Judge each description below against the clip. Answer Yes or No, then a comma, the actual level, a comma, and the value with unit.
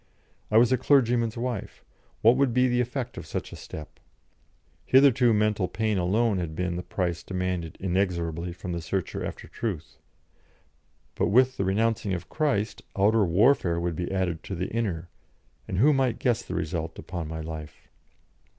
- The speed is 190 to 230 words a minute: No, average, 170 wpm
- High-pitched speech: No, very low, 95 Hz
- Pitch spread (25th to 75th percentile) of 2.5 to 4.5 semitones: No, wide, 5.4 semitones